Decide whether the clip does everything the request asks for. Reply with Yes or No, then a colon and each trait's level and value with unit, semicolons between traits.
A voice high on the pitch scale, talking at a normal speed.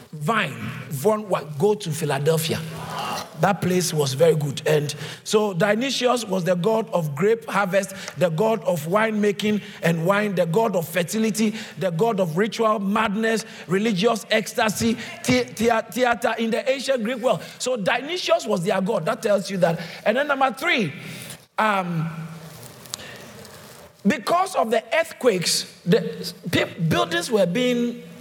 Yes: high, 210 Hz; average, 145 wpm